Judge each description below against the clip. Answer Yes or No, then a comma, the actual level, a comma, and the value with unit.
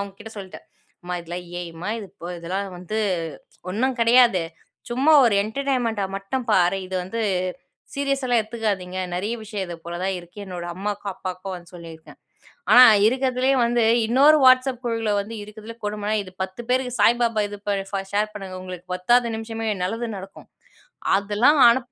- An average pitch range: Yes, average, 4.2 semitones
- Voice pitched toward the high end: Yes, high, 210 Hz